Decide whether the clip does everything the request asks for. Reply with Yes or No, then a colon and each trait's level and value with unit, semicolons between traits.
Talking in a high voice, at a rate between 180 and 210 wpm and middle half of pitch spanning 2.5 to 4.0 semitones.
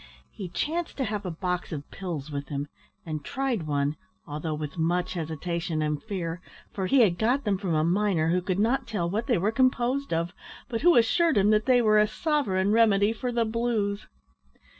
No: high, 195 Hz; average, 195 wpm; wide, 5.6 semitones